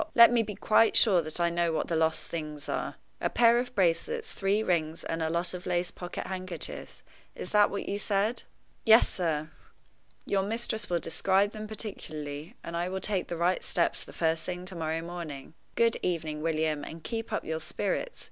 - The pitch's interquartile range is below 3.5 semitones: No, average, 4.3 semitones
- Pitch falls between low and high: Yes, medium, 175 Hz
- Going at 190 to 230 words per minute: Yes, average, 195 wpm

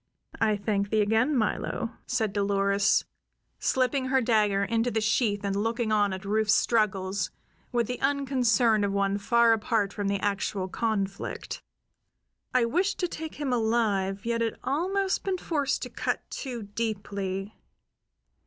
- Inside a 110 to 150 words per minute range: Yes, average, 145 wpm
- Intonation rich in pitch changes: No, average, 3.6 semitones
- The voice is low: No, high, 220 Hz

